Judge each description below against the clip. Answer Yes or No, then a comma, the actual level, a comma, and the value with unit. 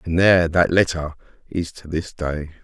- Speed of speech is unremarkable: Yes, average, 180 wpm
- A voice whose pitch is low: Yes, very low, 80 Hz